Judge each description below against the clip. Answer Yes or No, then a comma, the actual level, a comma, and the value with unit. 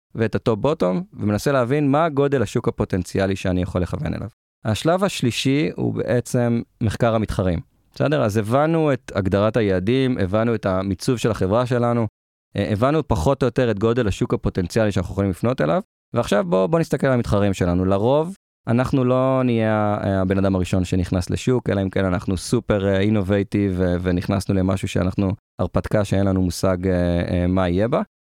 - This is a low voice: Yes, low, 105 Hz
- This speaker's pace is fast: Yes, fast, 155 wpm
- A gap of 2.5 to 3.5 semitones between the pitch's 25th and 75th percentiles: No, average, 4.6 semitones